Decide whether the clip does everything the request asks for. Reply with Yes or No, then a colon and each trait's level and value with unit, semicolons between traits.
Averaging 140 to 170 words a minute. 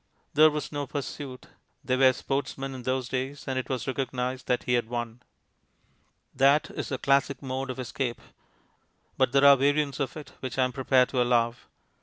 No: average, 185 wpm